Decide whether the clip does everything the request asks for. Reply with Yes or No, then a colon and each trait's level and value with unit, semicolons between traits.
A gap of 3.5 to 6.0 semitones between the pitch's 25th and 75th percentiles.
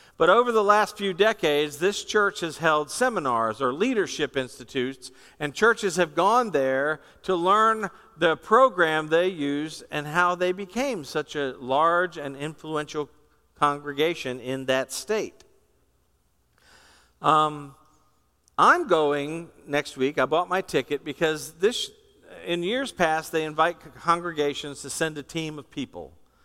Yes: average, 4.7 semitones